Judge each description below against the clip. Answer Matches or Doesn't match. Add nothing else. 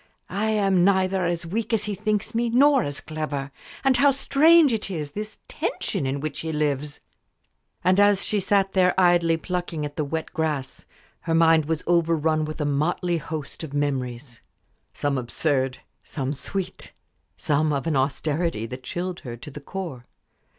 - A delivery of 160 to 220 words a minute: Matches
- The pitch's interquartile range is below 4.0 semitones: Doesn't match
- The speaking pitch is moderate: Matches